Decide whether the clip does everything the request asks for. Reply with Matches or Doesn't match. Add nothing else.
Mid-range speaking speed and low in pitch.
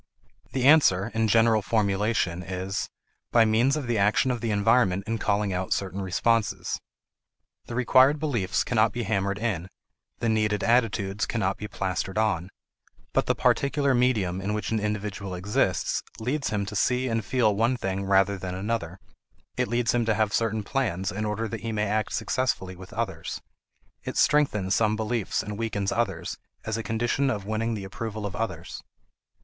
Matches